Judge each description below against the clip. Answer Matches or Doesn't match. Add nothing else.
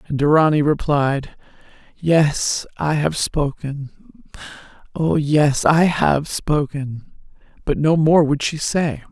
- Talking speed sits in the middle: Doesn't match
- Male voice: Doesn't match